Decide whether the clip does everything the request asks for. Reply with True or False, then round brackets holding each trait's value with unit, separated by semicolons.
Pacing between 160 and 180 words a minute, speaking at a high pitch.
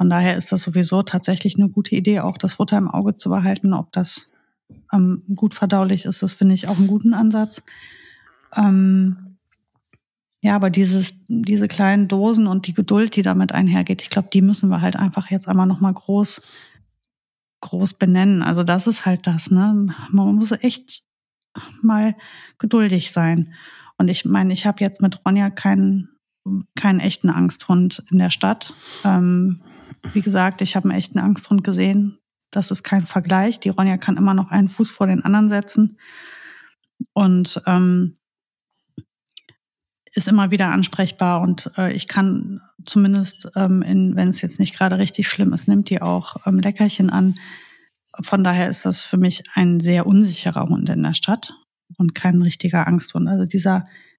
True (170 wpm; 195 Hz)